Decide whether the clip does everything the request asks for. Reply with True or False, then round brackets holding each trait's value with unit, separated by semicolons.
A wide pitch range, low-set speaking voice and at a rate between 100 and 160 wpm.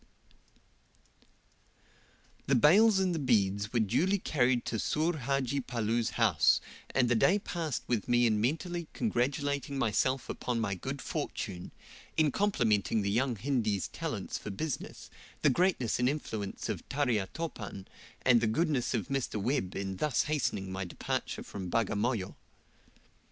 True (5.7 semitones; 125 Hz; 140 wpm)